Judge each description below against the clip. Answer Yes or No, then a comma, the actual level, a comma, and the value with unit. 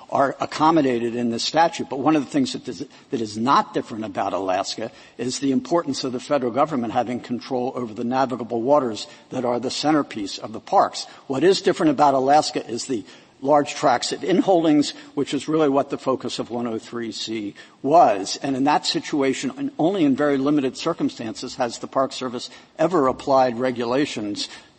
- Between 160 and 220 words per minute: Yes, average, 175 wpm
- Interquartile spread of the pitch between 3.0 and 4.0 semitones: Yes, average, 3.6 semitones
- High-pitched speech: No, low, 135 Hz